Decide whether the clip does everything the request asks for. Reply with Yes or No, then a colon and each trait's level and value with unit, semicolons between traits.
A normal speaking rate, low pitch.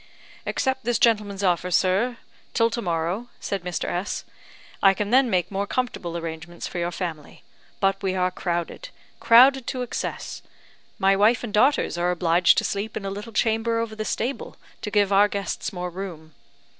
No: average, 175 wpm; high, 200 Hz